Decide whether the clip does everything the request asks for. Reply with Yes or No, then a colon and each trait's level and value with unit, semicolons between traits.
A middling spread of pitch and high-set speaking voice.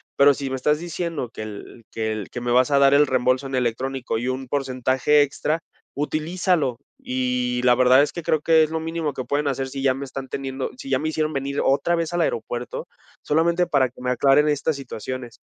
No: average, 3.0 semitones; low, 135 Hz